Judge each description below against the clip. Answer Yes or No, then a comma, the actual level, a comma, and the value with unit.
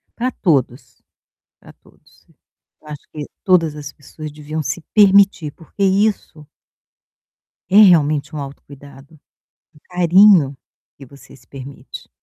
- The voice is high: No, medium, 155 Hz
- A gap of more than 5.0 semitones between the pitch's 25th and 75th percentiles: No, average, 4.3 semitones